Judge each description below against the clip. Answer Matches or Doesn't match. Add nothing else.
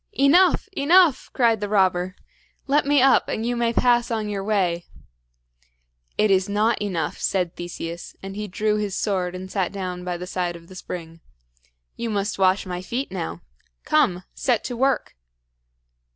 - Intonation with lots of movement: Doesn't match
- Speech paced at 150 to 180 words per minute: Matches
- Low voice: Doesn't match